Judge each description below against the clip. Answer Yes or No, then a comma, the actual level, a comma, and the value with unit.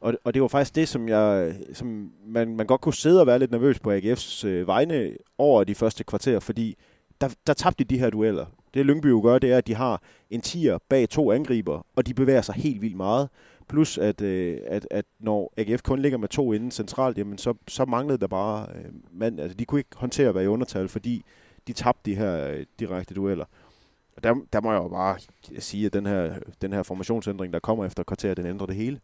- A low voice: Yes, low, 110 Hz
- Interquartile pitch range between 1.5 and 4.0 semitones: No, average, 4.5 semitones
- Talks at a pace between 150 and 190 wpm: No, fast, 225 wpm